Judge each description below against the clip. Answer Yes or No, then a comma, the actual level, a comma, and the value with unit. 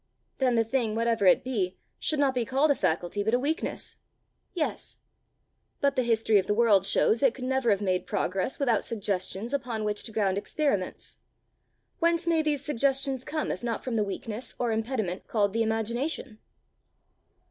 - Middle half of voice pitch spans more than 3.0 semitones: Yes, average, 4.5 semitones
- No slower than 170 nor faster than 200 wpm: Yes, average, 175 wpm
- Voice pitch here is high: Yes, high, 230 Hz